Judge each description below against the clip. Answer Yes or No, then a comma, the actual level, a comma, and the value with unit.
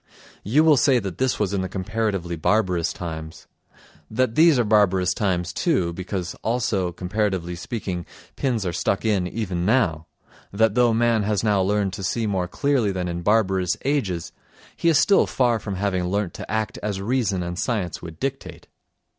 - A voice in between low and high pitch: No, low, 100 Hz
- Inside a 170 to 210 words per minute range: Yes, average, 175 wpm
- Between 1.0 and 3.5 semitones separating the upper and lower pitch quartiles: No, average, 4.1 semitones